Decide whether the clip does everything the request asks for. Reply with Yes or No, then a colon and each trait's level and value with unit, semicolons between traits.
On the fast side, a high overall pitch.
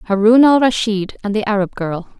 No: average, 190 wpm; high, 215 Hz